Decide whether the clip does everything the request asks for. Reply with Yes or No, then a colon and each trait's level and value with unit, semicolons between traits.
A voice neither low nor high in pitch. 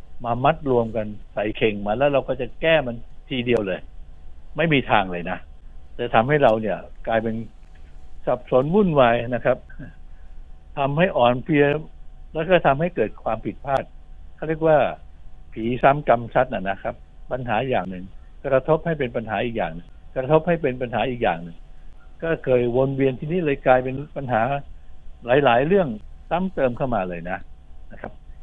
No: low, 115 Hz